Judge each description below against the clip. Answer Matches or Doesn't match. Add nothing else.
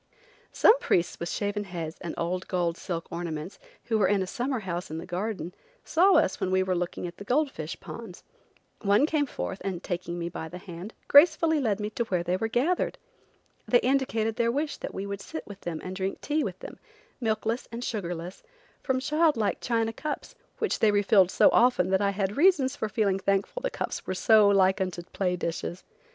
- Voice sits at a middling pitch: Doesn't match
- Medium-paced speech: Doesn't match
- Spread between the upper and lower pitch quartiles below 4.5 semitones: Doesn't match